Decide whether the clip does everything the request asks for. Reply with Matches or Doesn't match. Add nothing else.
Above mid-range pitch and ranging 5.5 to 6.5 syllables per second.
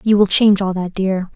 Matches